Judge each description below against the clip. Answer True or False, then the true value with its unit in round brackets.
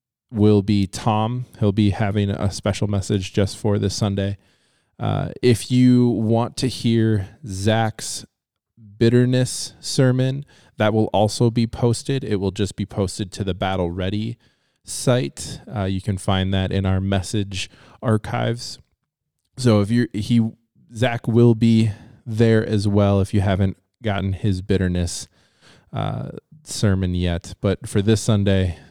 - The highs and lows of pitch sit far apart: False (3.0 semitones)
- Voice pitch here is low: True (105 Hz)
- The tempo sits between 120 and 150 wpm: True (145 wpm)